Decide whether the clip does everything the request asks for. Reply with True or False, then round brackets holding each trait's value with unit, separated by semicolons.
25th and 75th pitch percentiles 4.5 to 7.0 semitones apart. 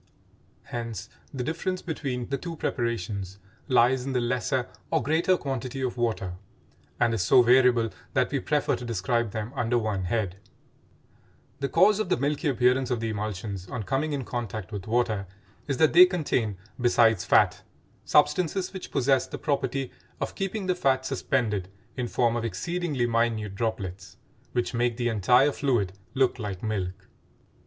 False (3.9 semitones)